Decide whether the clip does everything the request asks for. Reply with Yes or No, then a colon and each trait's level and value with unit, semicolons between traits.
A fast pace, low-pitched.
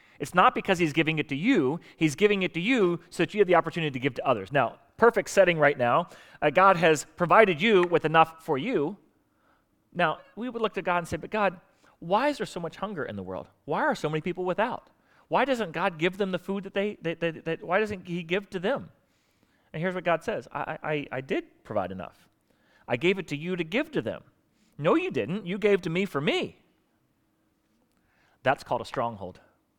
No: fast, 230 wpm; medium, 180 Hz